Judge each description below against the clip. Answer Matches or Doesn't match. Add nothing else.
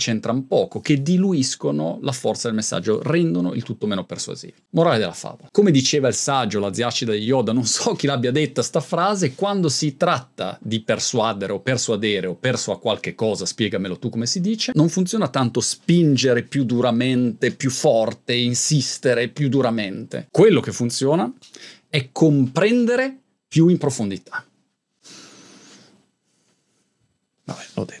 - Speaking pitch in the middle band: Doesn't match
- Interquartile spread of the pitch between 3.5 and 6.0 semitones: Matches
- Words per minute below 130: Doesn't match